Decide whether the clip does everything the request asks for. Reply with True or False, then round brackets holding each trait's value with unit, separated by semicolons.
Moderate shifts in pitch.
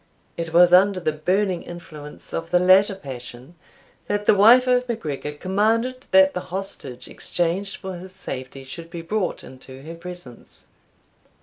True (4.3 semitones)